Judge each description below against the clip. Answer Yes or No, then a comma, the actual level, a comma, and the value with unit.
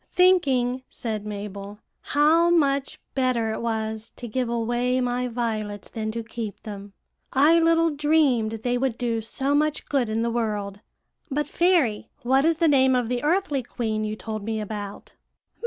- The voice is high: Yes, high, 240 Hz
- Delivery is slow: No, average, 165 wpm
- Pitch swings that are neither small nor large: Yes, average, 4.3 semitones